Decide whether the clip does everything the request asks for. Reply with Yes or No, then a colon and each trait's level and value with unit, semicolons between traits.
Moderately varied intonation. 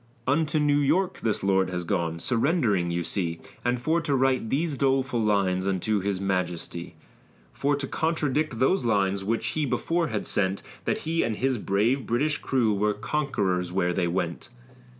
No: wide, 6.9 semitones